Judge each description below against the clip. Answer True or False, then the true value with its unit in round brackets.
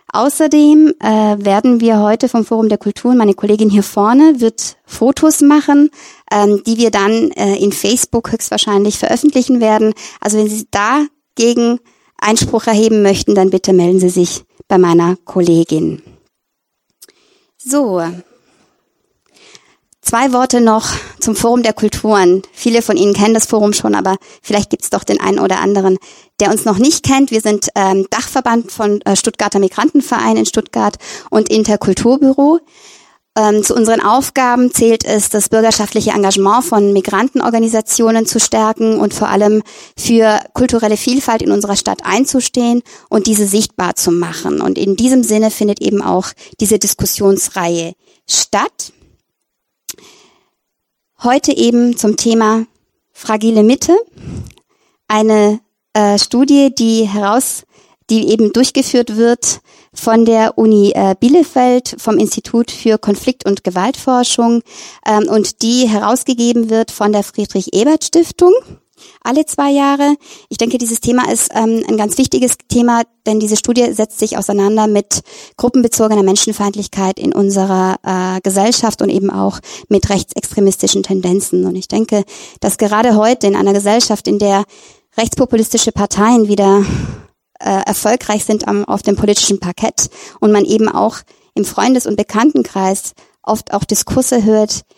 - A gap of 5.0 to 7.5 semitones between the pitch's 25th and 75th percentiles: False (3.2 semitones)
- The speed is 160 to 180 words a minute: False (140 wpm)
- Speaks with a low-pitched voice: False (220 Hz)